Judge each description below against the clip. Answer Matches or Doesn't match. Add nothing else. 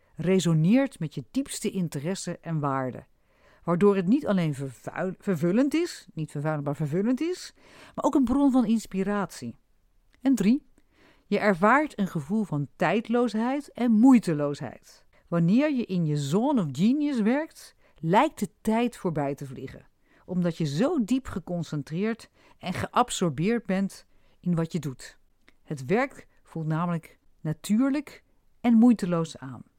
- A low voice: Doesn't match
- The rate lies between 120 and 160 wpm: Matches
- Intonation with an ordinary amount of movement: Doesn't match